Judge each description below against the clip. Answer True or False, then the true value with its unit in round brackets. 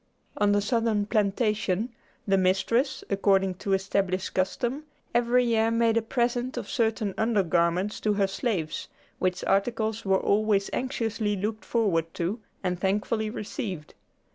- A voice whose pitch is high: True (210 Hz)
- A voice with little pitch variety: False (3.1 semitones)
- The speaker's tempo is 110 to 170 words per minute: True (140 wpm)